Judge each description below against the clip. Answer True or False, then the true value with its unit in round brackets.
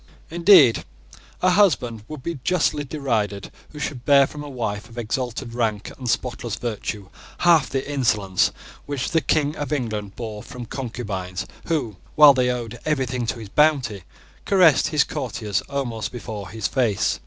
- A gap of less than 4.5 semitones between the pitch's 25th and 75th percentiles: False (4.9 semitones)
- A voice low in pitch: True (125 Hz)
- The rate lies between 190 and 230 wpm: False (155 wpm)